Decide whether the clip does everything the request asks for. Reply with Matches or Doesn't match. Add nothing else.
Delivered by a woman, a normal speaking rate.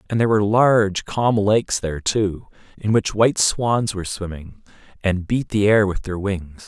Doesn't match